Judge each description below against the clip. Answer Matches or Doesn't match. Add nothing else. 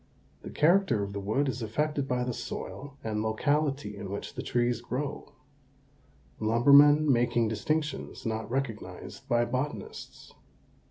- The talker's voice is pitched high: Doesn't match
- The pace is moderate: Doesn't match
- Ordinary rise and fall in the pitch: Matches